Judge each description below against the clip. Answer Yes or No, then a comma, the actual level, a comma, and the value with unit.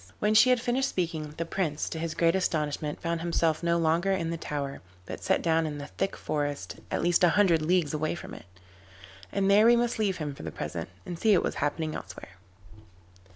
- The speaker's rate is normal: No, fast, 215 wpm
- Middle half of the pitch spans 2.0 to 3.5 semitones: No, average, 3.9 semitones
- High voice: No, medium, 165 Hz